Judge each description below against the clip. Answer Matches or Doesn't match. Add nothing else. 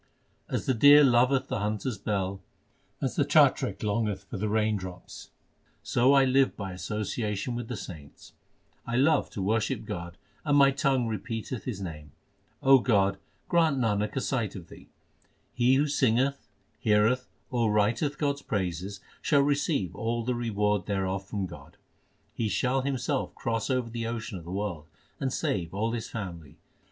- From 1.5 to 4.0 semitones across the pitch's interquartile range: Doesn't match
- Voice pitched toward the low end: Matches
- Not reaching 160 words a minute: Doesn't match